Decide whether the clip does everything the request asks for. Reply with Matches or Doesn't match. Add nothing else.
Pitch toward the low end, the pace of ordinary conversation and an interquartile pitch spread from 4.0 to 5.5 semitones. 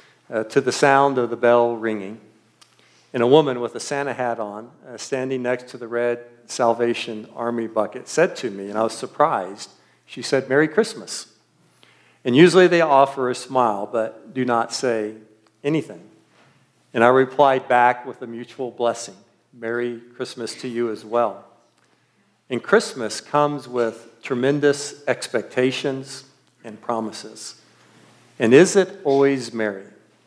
Doesn't match